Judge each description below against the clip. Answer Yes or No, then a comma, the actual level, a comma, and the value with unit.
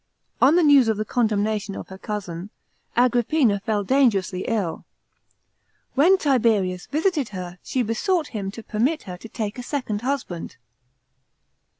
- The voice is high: Yes, high, 225 Hz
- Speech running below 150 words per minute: Yes, average, 140 wpm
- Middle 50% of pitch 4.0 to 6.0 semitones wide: Yes, average, 5.1 semitones